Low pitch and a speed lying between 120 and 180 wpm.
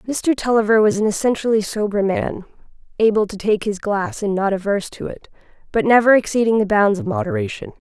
No: high, 215 Hz; average, 175 wpm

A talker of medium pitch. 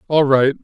Yes: medium, 145 Hz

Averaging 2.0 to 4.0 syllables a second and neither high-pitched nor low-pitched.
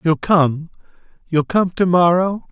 Yes: 3.9 syllables/s; medium, 170 Hz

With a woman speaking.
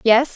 Yes: female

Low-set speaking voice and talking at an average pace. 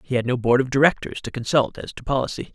No: low, 130 Hz; fast, 260 wpm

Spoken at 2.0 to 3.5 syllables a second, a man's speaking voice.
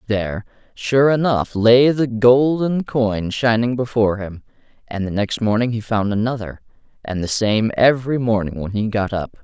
No: 4.8 syllables/s; male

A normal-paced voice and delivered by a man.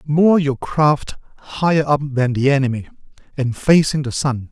Yes: average, 160 wpm; male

